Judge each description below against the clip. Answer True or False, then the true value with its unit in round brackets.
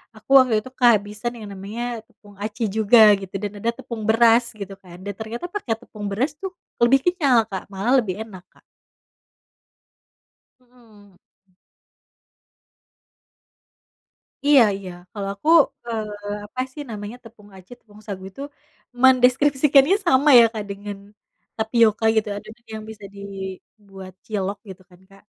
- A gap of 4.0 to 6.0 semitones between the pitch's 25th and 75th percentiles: False (3.4 semitones)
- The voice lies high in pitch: True (215 Hz)